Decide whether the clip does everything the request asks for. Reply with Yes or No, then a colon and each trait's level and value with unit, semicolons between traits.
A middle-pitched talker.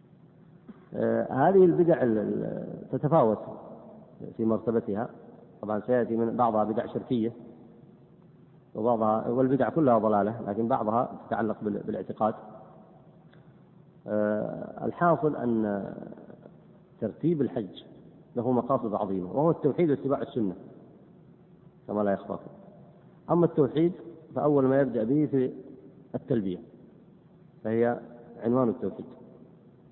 No: low, 130 Hz